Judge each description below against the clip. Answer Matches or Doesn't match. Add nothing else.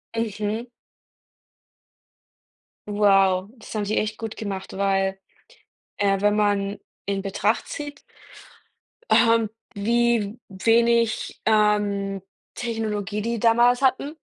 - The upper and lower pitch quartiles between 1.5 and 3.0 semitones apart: Matches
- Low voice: Doesn't match